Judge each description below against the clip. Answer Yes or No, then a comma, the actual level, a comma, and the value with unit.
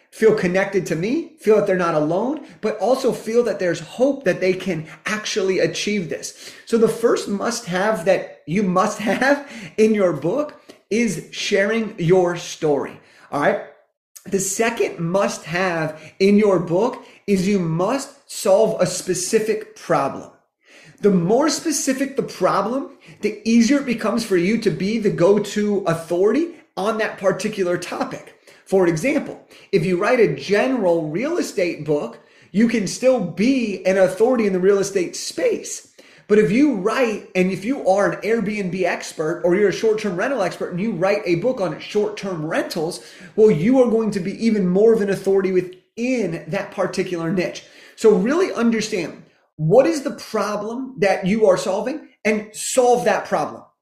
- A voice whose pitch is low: No, high, 205 Hz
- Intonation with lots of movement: No, average, 3.8 semitones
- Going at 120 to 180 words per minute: Yes, average, 165 wpm